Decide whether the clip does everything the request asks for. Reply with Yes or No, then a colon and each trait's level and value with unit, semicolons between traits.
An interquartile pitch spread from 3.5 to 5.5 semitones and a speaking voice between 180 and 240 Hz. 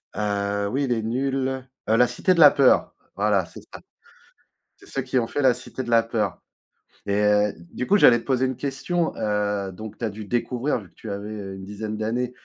No: average, 4.1 semitones; low, 115 Hz